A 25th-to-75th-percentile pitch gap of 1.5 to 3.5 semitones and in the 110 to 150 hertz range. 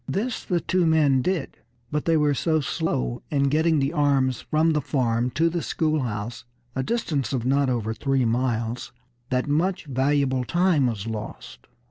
No: average, 4.1 semitones; medium, 140 Hz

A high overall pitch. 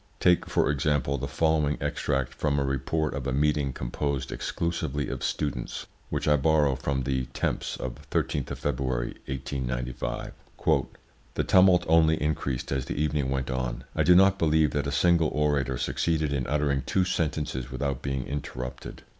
No: very low, 70 Hz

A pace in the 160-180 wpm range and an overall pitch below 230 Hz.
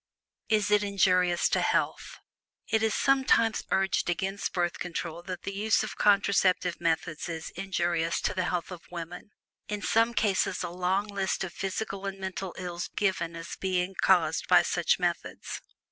Yes: average, 175 wpm; high, 190 Hz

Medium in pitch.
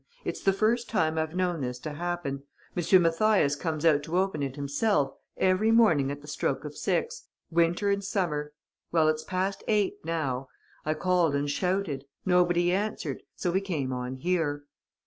Yes: medium, 170 Hz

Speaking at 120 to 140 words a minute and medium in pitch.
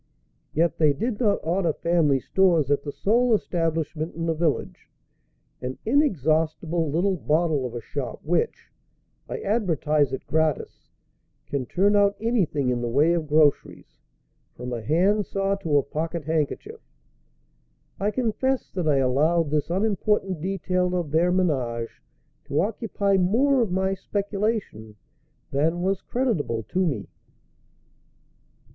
Yes: slow, 135 wpm; medium, 165 Hz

